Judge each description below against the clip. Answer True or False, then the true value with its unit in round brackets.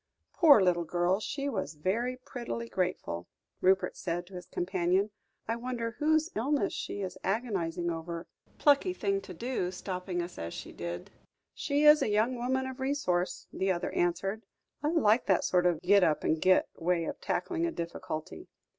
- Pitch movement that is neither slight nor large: False (6.1 semitones)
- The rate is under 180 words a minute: True (170 wpm)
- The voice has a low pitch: False (190 Hz)